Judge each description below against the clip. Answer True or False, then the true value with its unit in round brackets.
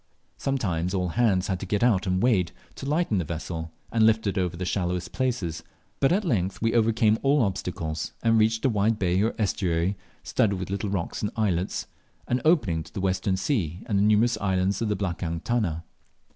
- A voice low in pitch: True (100 Hz)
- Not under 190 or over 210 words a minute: True (200 wpm)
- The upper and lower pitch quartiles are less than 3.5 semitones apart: False (3.9 semitones)